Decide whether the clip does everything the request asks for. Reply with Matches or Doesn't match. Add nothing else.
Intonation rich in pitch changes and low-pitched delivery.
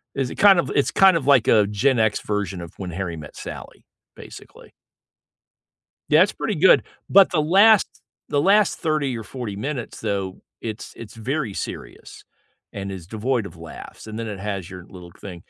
Matches